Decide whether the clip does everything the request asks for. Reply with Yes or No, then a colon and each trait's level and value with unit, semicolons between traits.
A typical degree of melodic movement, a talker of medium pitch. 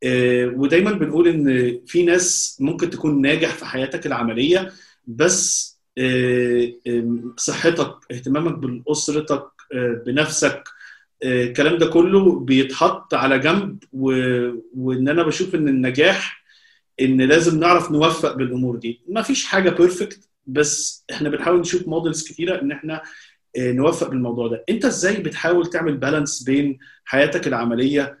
Yes: average, 4.9 semitones; medium, 150 Hz